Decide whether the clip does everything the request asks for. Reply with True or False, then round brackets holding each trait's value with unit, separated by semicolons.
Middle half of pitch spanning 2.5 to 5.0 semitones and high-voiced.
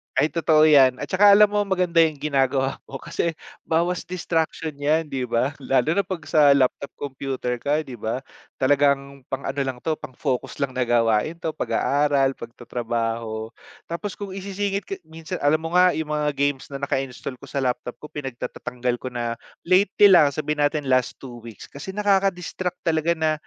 False (4.5 semitones; 145 Hz)